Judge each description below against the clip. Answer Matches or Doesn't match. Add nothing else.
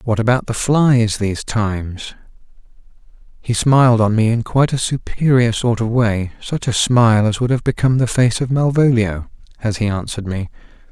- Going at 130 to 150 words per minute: Doesn't match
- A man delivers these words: Matches